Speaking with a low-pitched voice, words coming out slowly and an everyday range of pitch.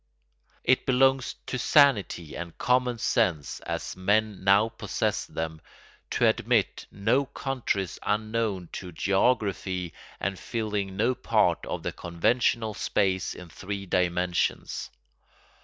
Yes: low, 100 Hz; slow, 115 wpm; average, 4.5 semitones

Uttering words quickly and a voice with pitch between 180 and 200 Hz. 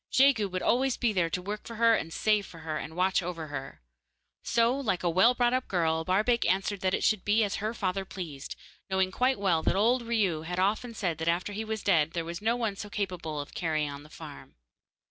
Yes: fast, 235 wpm; high, 190 Hz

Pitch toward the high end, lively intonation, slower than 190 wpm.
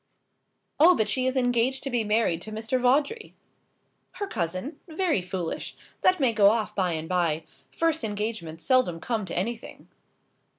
Yes: high, 225 Hz; wide, 6.3 semitones; average, 160 wpm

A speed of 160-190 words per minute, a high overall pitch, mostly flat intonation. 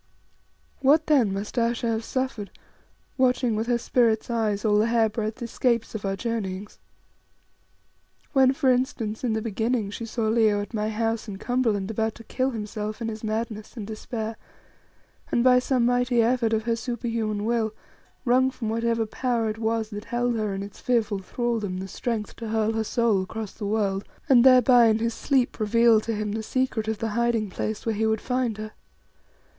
Yes: average, 185 wpm; high, 225 Hz; narrow, 1.9 semitones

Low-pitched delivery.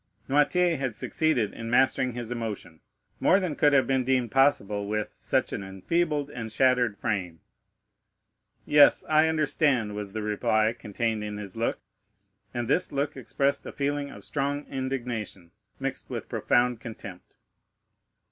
Yes: low, 125 Hz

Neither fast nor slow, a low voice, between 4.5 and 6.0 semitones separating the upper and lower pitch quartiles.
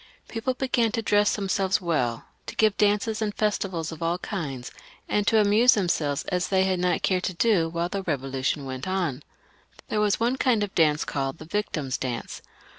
No: average, 190 wpm; medium, 185 Hz; average, 5.2 semitones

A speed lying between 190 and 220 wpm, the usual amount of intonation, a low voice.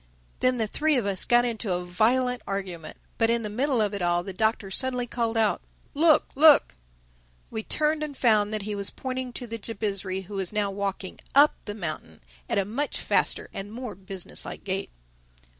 No: average, 195 wpm; average, 4.2 semitones; high, 215 Hz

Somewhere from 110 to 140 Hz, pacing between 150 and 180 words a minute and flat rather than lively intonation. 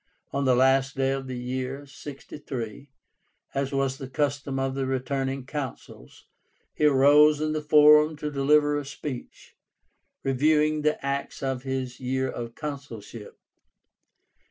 No: low, 135 Hz; slow, 135 wpm; narrow, 1.9 semitones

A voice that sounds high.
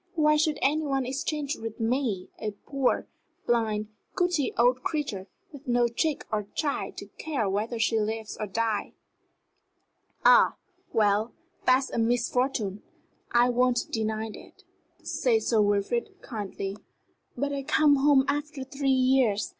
Yes: high, 245 Hz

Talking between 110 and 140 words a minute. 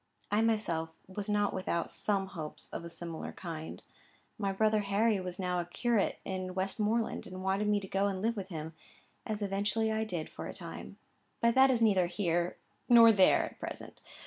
No: average, 190 wpm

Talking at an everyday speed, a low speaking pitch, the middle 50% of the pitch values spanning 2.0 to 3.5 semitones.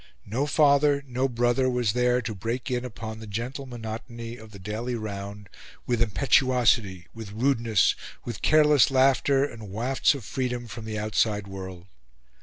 Yes: average, 155 wpm; low, 120 Hz; average, 3.2 semitones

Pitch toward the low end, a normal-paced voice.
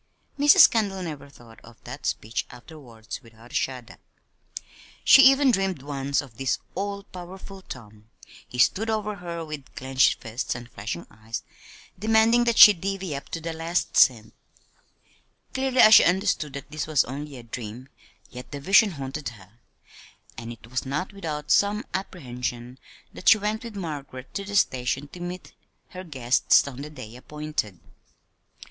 No: medium, 150 Hz; average, 160 wpm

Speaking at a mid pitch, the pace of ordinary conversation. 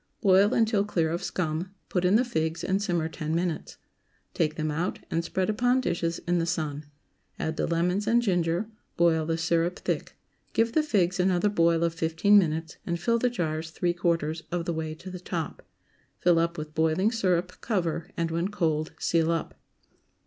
Yes: medium, 170 Hz; average, 185 wpm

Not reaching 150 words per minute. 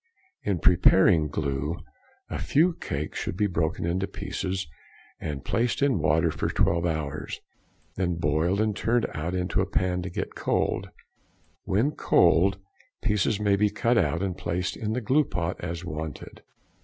No: average, 155 wpm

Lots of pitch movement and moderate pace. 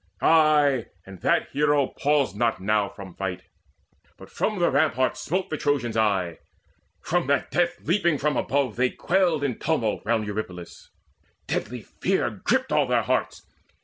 Yes: wide, 6.2 semitones; average, 150 wpm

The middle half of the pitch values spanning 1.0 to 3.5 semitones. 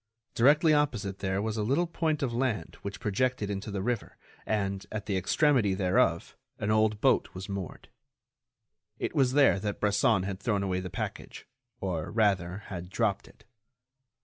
No: average, 3.9 semitones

